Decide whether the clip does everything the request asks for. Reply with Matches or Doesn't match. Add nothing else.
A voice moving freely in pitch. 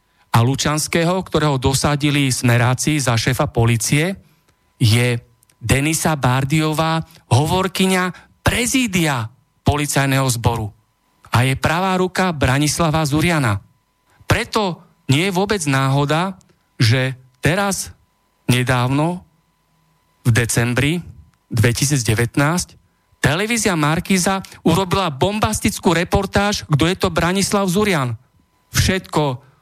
Matches